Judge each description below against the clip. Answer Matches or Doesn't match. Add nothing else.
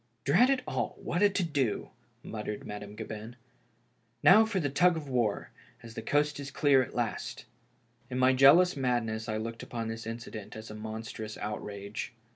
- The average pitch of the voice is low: Matches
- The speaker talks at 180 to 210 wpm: Matches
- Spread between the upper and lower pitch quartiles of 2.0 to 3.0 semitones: Doesn't match